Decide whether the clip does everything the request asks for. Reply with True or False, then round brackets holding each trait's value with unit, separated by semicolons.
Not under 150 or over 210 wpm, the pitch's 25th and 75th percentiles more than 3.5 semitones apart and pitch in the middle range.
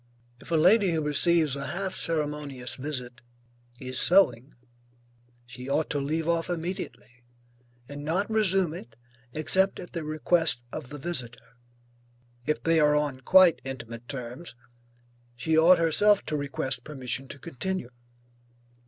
False (135 wpm; 4.7 semitones; 150 Hz)